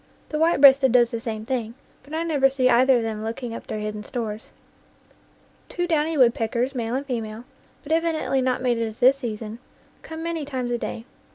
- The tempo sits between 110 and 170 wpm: No, average, 195 wpm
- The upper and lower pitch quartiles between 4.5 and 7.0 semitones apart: No, average, 3.8 semitones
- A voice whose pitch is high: Yes, very high, 250 Hz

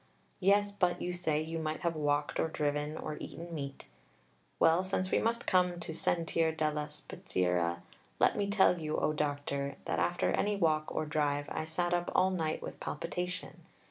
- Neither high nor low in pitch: Yes, medium, 160 Hz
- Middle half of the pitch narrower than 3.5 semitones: Yes, average, 3.1 semitones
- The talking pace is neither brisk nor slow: Yes, average, 175 wpm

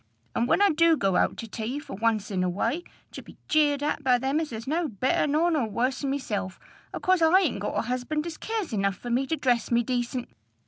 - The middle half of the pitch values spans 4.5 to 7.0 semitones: Yes, average, 5.3 semitones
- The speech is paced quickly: Yes, fast, 240 wpm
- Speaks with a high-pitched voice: Yes, very high, 260 Hz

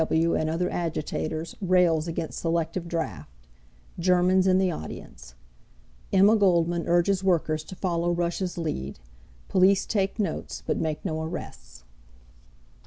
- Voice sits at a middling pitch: Yes, medium, 170 Hz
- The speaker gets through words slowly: Yes, slow, 130 wpm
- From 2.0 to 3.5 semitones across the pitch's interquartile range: Yes, narrow, 2.5 semitones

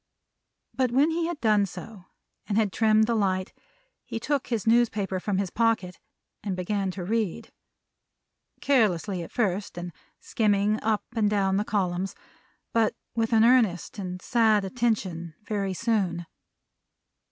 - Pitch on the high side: Yes, high, 210 Hz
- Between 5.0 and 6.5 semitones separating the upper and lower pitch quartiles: No, average, 3.3 semitones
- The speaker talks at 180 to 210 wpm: No, average, 145 wpm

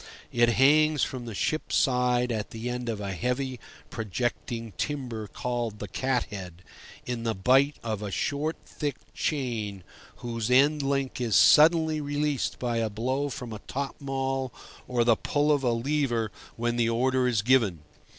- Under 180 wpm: Yes, average, 165 wpm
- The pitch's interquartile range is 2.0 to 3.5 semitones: Yes, average, 3.2 semitones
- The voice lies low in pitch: Yes, low, 125 Hz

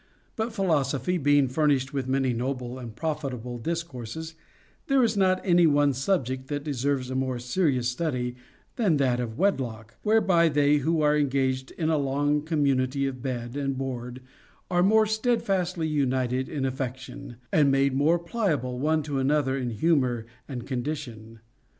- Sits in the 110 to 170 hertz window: Yes, medium, 140 Hz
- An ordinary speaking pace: Yes, average, 155 wpm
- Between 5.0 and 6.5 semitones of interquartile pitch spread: No, average, 3.8 semitones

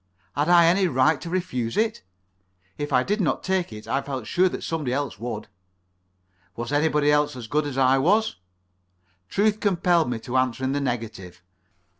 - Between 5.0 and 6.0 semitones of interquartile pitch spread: Yes, wide, 5.6 semitones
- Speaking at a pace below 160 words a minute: No, average, 180 wpm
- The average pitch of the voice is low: No, medium, 145 Hz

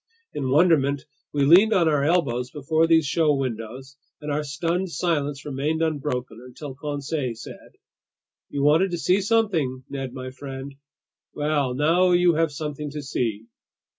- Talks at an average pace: Yes, average, 150 wpm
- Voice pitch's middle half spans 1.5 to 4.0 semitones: Yes, average, 3.4 semitones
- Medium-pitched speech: Yes, medium, 145 Hz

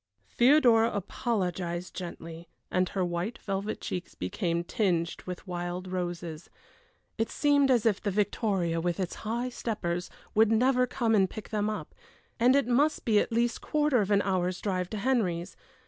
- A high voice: Yes, high, 200 Hz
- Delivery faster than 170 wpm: No, average, 165 wpm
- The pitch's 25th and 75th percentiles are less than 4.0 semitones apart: No, average, 4.7 semitones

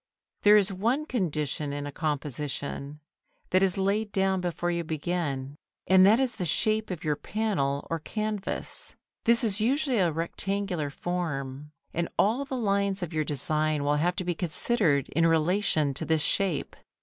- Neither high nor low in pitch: Yes, medium, 175 Hz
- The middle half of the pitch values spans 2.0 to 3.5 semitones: No, average, 5.2 semitones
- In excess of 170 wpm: No, average, 165 wpm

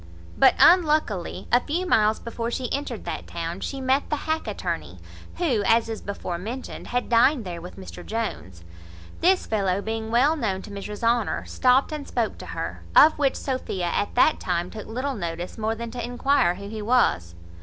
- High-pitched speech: Yes, high, 230 Hz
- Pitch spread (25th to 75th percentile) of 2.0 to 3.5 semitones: No, average, 5.1 semitones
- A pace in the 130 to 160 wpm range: No, average, 185 wpm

